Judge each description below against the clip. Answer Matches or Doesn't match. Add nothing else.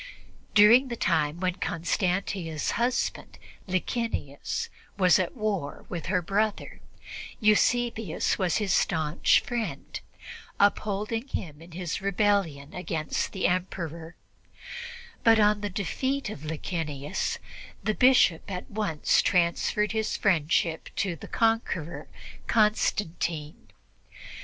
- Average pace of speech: Doesn't match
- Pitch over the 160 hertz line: Matches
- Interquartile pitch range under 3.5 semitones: Doesn't match